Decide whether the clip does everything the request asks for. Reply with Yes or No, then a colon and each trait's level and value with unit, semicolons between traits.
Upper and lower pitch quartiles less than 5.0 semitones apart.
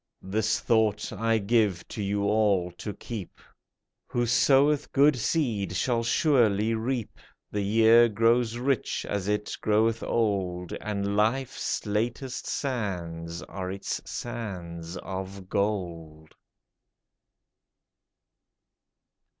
Yes: average, 3.3 semitones